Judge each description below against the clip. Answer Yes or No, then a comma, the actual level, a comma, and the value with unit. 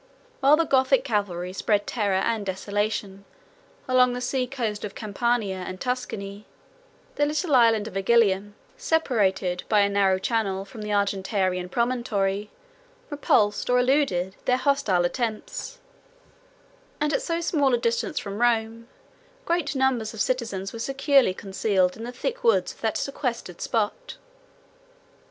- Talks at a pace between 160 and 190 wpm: No, average, 140 wpm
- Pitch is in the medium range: No, high, 225 Hz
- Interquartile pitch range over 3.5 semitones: Yes, average, 4.5 semitones